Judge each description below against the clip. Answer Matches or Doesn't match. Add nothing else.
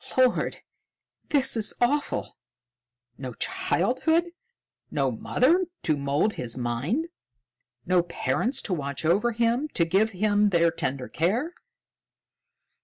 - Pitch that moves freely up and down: Matches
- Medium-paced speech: Doesn't match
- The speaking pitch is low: Doesn't match